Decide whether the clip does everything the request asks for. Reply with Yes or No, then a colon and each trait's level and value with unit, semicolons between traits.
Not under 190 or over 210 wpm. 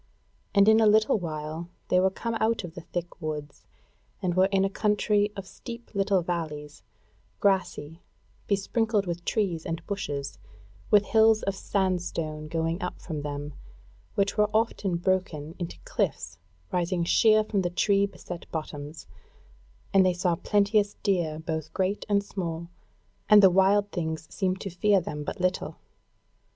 No: average, 155 wpm